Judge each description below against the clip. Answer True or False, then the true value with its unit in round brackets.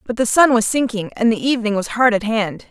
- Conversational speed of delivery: False (265 wpm)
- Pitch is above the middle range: True (225 Hz)